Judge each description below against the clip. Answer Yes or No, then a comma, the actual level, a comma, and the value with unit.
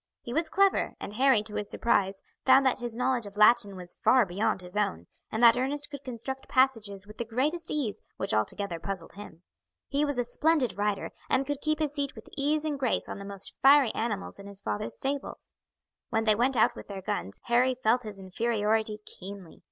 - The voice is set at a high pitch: Yes, high, 230 Hz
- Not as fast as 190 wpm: No, fast, 205 wpm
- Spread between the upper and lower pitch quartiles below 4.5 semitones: No, average, 4.9 semitones